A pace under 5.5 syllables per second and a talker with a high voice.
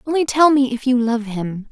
Yes: 5.0 syllables/s; very high, 250 Hz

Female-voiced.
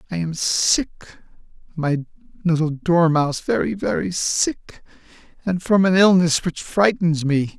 No: male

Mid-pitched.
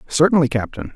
Yes: medium, 155 Hz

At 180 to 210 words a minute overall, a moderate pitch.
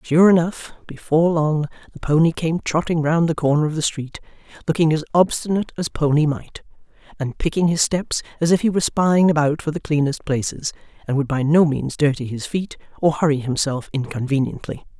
Yes: average, 185 wpm; medium, 155 Hz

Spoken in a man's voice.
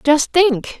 No: female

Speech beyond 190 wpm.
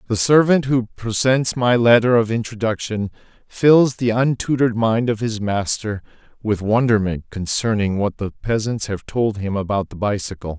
No: average, 155 wpm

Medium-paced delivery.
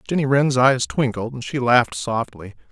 Yes: average, 175 wpm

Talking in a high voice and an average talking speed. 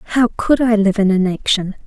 Yes: high, 210 Hz; average, 195 wpm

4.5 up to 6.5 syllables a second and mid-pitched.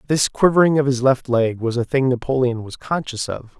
No: 5.3 syllables/s; low, 130 Hz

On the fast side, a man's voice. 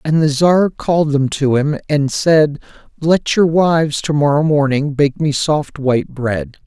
No: average, 180 wpm; male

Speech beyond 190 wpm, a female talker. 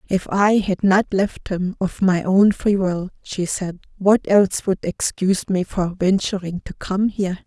No: average, 185 wpm; female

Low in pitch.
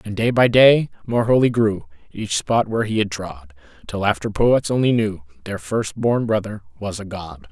Yes: low, 110 Hz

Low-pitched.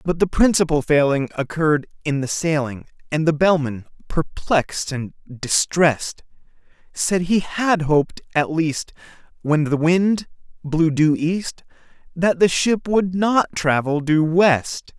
No: medium, 160 Hz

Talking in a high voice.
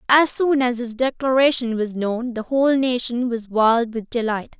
Yes: high, 245 Hz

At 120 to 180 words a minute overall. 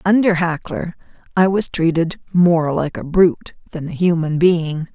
Yes: average, 160 wpm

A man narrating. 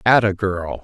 Yes: male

